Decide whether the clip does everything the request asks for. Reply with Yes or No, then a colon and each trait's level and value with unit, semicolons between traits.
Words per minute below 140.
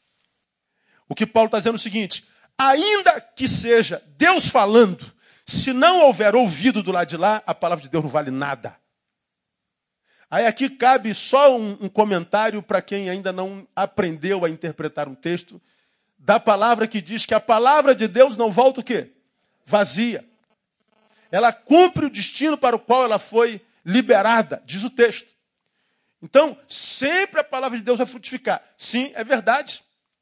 No: average, 165 wpm